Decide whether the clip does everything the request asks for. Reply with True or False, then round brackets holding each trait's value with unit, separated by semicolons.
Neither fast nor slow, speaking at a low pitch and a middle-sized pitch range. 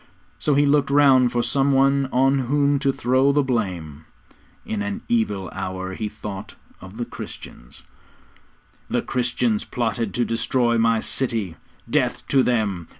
True (150 wpm; 120 Hz; 4.5 semitones)